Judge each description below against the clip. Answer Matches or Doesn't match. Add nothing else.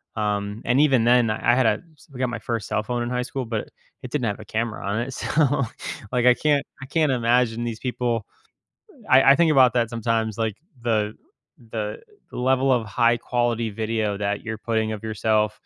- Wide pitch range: Doesn't match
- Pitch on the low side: Matches